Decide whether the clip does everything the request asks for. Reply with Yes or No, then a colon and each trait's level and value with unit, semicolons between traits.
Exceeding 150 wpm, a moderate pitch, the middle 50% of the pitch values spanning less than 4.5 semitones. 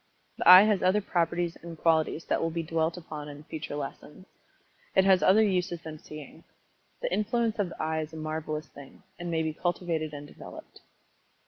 Yes: average, 190 wpm; medium, 165 Hz; average, 2.8 semitones